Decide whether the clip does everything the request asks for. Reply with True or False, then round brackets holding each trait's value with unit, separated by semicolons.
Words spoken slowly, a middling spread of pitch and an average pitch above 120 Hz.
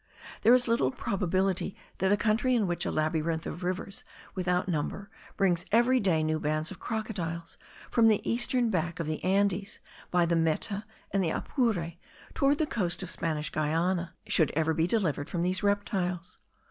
False (170 wpm; 4.2 semitones; 185 Hz)